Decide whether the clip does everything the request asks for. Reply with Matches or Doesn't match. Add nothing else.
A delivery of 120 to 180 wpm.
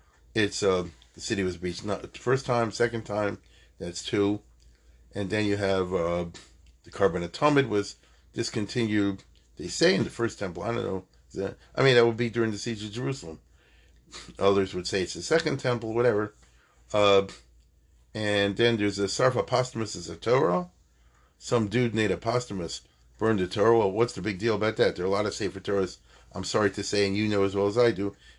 Doesn't match